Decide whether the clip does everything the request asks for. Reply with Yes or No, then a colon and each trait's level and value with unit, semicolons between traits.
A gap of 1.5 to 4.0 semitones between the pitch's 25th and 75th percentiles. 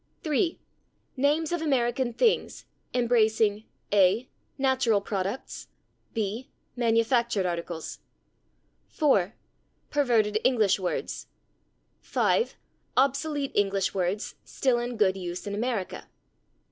No: average, 4.7 semitones